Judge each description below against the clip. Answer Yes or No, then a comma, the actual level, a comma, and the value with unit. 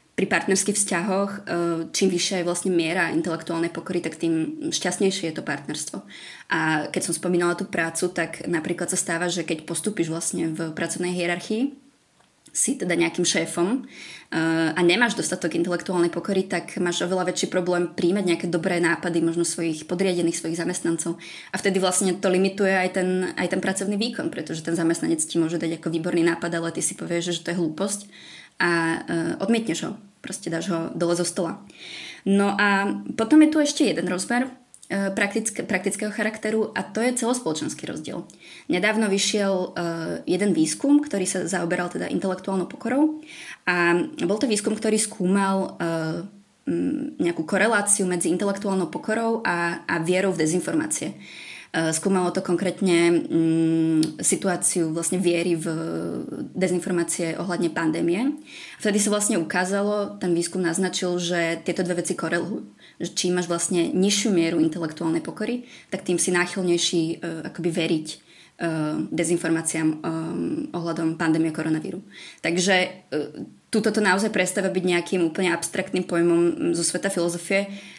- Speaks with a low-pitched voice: No, medium, 180 Hz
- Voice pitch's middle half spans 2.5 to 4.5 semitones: Yes, average, 2.8 semitones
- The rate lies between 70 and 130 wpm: No, average, 150 wpm